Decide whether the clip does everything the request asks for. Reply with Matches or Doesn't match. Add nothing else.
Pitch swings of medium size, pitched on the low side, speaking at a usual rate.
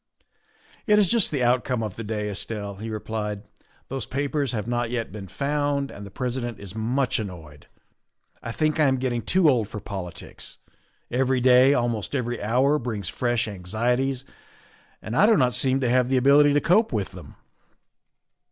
Matches